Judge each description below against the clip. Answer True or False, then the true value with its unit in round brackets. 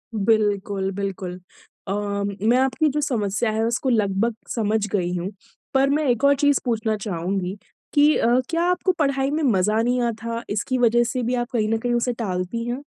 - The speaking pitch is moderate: False (230 Hz)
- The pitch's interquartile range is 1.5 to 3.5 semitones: False (4.3 semitones)